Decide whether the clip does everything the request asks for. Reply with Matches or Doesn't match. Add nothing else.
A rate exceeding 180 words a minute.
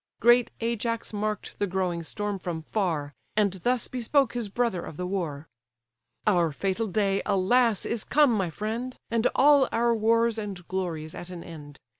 Doesn't match